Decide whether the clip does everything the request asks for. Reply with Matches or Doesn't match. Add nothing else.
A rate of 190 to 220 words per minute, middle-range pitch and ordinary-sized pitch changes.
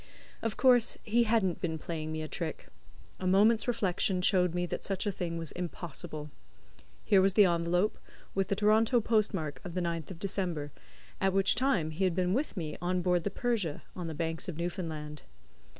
Matches